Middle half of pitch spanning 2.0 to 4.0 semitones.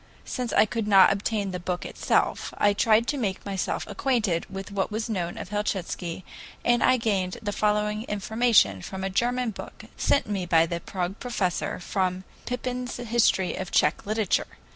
Yes: average, 3.5 semitones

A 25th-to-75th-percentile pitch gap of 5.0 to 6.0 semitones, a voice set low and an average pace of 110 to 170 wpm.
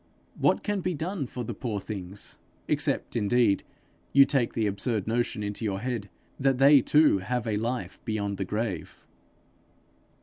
No: average, 4.1 semitones; low, 115 Hz; average, 160 wpm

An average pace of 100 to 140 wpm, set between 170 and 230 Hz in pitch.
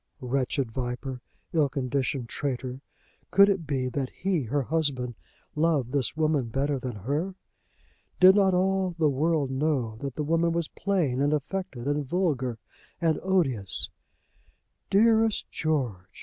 No: slow, 135 wpm; medium, 145 Hz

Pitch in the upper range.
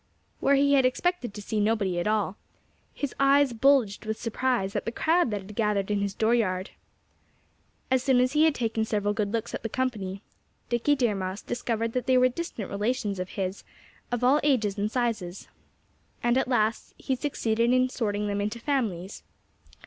Yes: high, 225 Hz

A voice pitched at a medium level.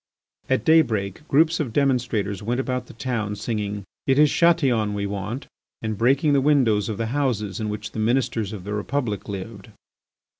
No: low, 115 Hz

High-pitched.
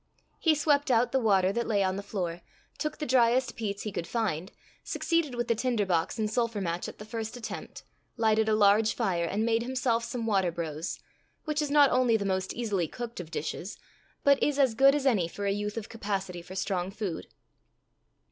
Yes: high, 220 Hz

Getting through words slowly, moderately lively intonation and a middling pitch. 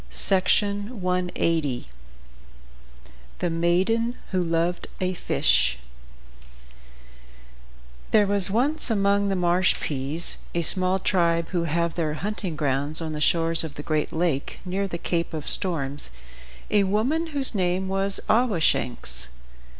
Yes: slow, 115 wpm; average, 3.6 semitones; medium, 180 Hz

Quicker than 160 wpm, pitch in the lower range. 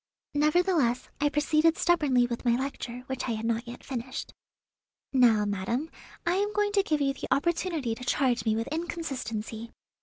No: average, 170 wpm; very high, 265 Hz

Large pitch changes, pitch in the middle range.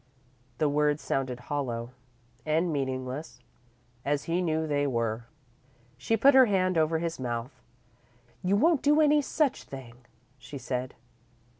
Yes: wide, 6.0 semitones; medium, 145 Hz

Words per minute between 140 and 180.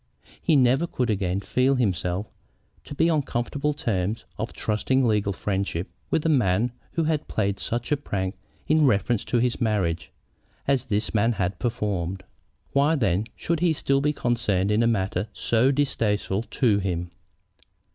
Yes: average, 160 wpm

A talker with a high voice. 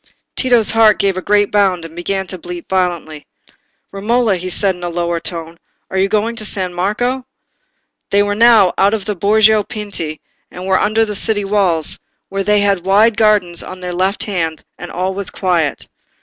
Yes: high, 195 Hz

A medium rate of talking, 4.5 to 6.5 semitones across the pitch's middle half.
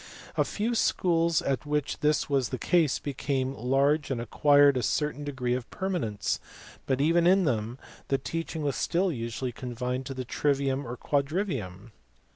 No: average, 160 wpm; average, 3.4 semitones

